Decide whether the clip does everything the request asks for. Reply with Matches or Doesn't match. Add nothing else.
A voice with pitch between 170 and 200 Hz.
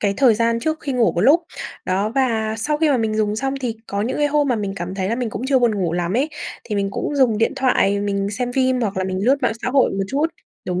Doesn't match